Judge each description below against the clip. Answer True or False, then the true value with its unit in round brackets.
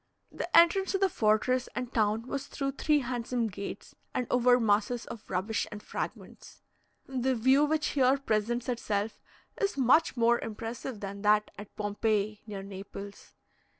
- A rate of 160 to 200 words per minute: False (150 wpm)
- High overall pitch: True (235 Hz)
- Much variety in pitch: False (3.8 semitones)